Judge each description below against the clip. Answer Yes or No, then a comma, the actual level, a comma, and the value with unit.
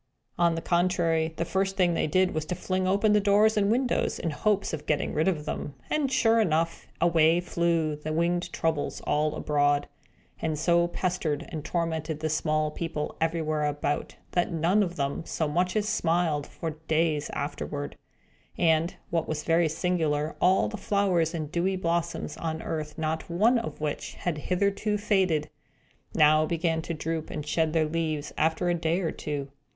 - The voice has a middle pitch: Yes, medium, 165 Hz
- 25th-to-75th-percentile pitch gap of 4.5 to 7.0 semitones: No, narrow, 2.6 semitones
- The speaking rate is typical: Yes, average, 180 wpm